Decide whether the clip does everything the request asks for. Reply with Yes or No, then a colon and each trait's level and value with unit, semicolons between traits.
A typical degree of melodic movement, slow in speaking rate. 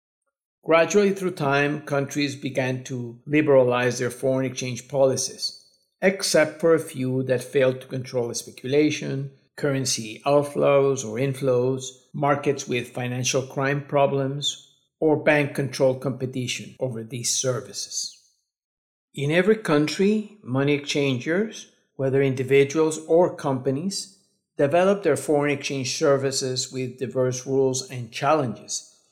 No: narrow, 2.3 semitones; slow, 115 wpm